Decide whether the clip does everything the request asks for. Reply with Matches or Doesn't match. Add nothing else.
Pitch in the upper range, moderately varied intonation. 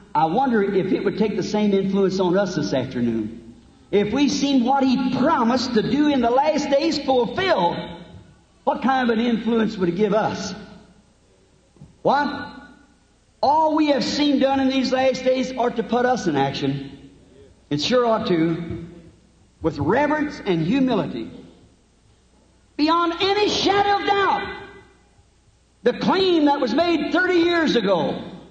Doesn't match